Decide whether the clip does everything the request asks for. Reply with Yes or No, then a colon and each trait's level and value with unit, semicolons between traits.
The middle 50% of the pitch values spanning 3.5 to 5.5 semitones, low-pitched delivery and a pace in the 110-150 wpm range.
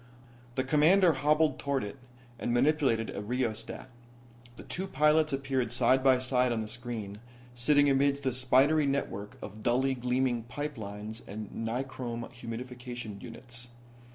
No: average, 3.0 semitones; low, 125 Hz; average, 140 wpm